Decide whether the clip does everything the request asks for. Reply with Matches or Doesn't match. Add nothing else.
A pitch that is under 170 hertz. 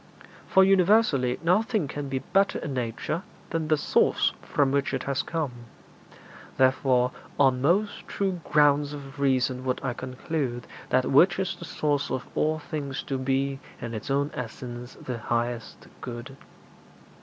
Matches